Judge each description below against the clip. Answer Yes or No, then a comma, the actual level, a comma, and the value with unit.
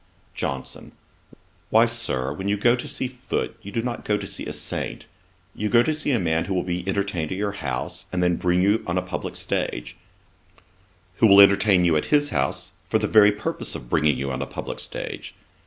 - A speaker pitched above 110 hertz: No, low, 100 Hz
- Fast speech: Yes, fast, 215 wpm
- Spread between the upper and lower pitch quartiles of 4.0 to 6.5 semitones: Yes, average, 4.5 semitones